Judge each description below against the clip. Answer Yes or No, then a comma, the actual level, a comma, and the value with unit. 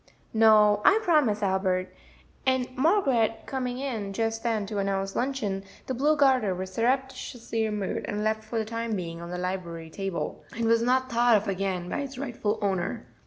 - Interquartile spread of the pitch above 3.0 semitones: Yes, average, 4.6 semitones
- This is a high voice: Yes, high, 220 Hz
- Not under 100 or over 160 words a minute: No, average, 175 wpm